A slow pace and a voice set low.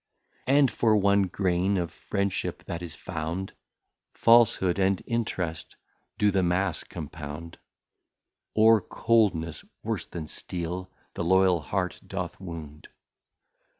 Yes: slow, 120 wpm; very low, 95 Hz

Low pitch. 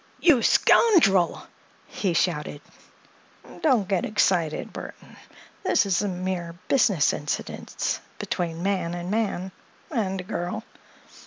No: high, 190 Hz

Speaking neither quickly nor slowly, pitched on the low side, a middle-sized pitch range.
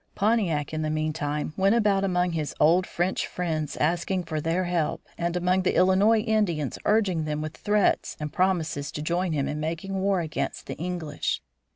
No: average, 180 wpm; medium, 175 Hz; average, 3.5 semitones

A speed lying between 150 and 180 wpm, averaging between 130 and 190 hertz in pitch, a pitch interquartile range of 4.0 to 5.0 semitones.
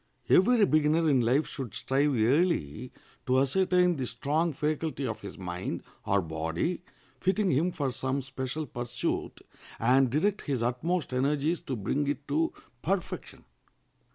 No: average, 140 wpm; medium, 140 Hz; average, 4.6 semitones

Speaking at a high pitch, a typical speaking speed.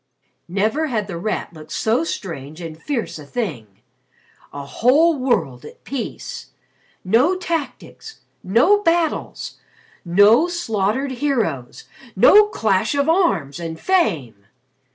No: high, 220 Hz; slow, 115 wpm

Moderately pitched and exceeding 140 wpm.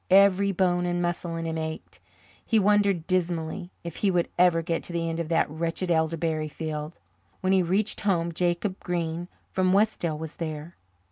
Yes: medium, 175 Hz; average, 180 wpm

